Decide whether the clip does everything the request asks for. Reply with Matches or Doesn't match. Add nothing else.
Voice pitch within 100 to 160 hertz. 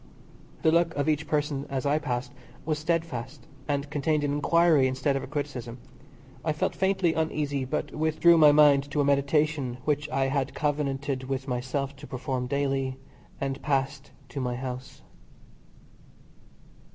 Matches